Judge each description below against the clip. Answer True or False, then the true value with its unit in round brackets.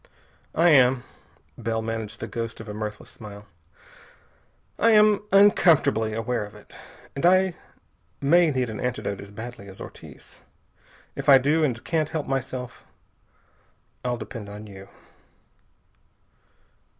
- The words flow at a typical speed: False (130 wpm)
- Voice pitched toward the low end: True (120 Hz)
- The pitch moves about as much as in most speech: False (6.0 semitones)